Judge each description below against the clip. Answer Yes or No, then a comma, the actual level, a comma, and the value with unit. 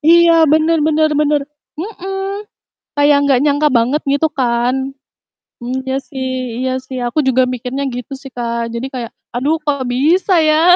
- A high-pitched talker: Yes, very high, 275 Hz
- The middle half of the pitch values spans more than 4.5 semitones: No, average, 3.6 semitones